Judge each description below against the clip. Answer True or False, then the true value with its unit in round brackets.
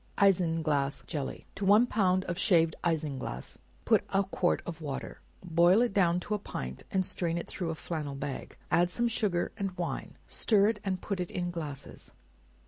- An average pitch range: True (3.6 semitones)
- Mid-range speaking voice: True (175 Hz)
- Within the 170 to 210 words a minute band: True (180 wpm)